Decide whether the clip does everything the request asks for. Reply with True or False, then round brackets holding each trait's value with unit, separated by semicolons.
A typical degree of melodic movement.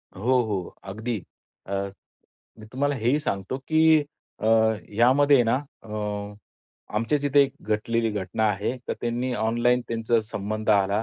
True (3.2 semitones)